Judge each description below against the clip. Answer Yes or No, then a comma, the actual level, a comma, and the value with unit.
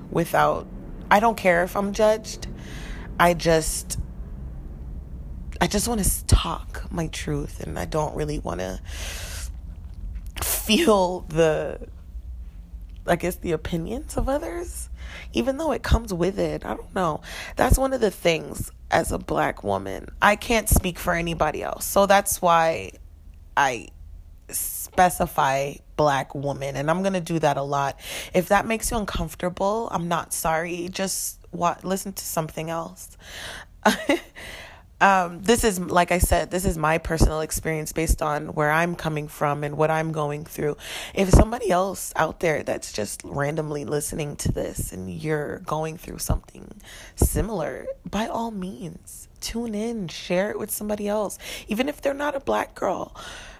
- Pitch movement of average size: No, wide, 7.7 semitones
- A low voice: No, medium, 160 Hz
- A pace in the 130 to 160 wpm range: Yes, average, 155 wpm